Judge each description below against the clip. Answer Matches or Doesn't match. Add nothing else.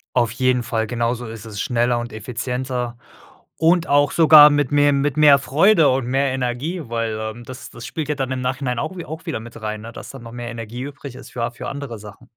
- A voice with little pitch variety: Doesn't match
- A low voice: Matches